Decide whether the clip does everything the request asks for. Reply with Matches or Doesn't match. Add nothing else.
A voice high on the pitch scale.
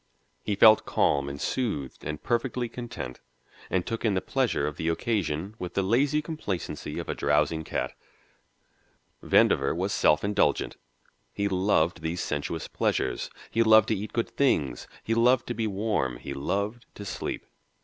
Doesn't match